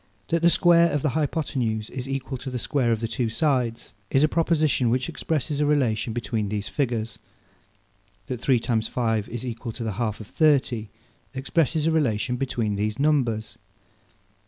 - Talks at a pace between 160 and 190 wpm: Yes, average, 175 wpm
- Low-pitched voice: Yes, low, 125 Hz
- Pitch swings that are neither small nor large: Yes, average, 4.5 semitones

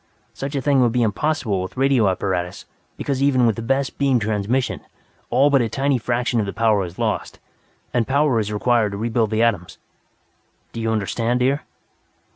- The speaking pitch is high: No, low, 115 Hz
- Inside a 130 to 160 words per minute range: No, average, 185 wpm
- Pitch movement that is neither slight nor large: Yes, average, 4.0 semitones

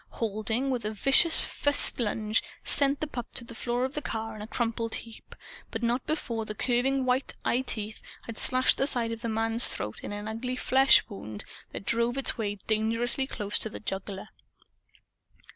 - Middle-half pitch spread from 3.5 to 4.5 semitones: No, average, 2.9 semitones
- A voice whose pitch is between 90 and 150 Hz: No, high, 230 Hz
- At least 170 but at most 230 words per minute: Yes, average, 185 wpm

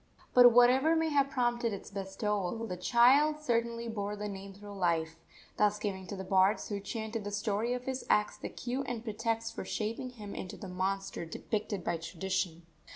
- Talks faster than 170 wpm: Yes, average, 185 wpm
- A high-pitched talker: Yes, high, 210 Hz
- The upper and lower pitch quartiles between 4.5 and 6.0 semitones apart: No, average, 3.6 semitones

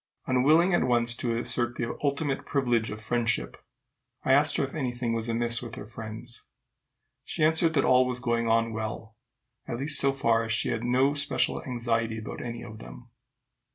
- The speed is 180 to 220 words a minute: Yes, average, 190 wpm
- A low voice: Yes, low, 120 Hz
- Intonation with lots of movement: No, average, 2.7 semitones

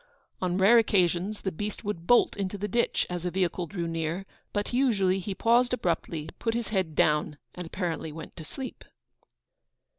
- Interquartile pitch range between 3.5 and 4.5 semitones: Yes, average, 3.8 semitones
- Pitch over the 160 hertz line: Yes, high, 190 Hz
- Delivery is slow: No, average, 175 wpm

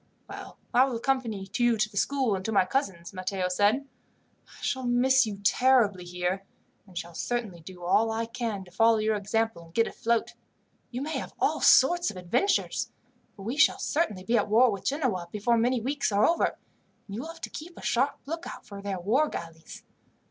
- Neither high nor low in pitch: No, high, 225 Hz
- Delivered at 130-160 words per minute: No, average, 200 wpm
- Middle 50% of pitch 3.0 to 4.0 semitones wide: No, average, 5.1 semitones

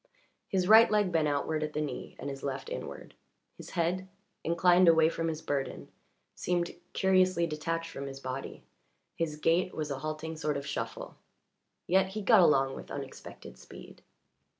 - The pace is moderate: Yes, average, 165 wpm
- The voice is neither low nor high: Yes, medium, 165 Hz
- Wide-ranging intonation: No, average, 3.2 semitones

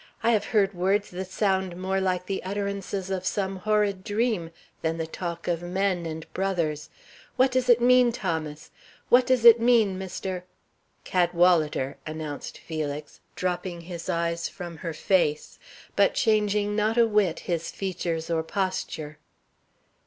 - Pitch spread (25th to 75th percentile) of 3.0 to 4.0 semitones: Yes, average, 3.6 semitones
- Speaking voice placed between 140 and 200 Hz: Yes, medium, 185 Hz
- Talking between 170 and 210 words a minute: No, average, 150 wpm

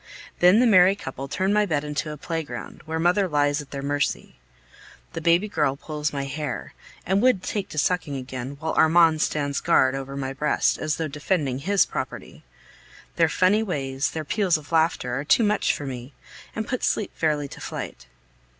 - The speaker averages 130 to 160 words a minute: No, average, 185 wpm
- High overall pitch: No, medium, 155 Hz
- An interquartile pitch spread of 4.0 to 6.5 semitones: Yes, average, 4.4 semitones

